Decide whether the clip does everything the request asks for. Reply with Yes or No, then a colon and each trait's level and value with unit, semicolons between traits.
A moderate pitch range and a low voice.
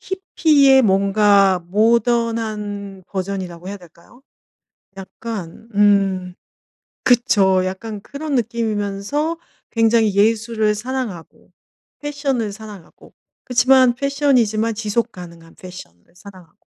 No: average, 3.8 semitones; high, 215 Hz